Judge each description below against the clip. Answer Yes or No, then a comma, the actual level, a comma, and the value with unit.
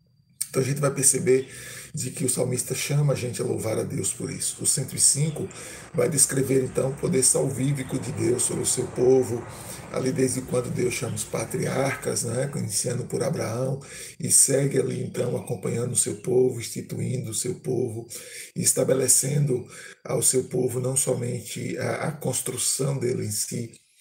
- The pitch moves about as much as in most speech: No, narrow, 1.6 semitones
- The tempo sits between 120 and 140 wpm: No, average, 165 wpm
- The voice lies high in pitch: No, low, 130 Hz